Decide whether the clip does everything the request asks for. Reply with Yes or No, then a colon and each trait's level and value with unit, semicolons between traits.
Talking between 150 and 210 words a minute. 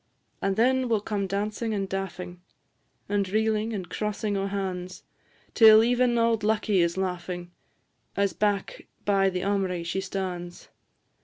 No: average, 140 wpm